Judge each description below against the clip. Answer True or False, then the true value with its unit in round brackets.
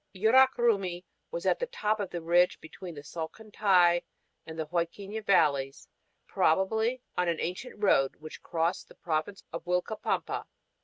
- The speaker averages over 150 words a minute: False (140 wpm)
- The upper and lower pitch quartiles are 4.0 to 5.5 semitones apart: True (4.4 semitones)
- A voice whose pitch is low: False (180 Hz)